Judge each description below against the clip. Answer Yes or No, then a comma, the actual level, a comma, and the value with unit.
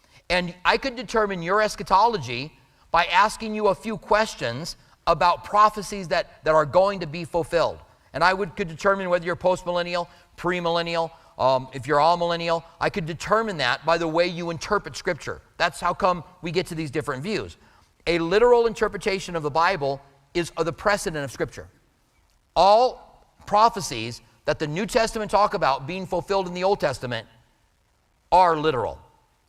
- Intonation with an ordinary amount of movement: Yes, average, 4.4 semitones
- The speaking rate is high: No, average, 165 wpm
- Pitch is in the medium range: Yes, medium, 175 Hz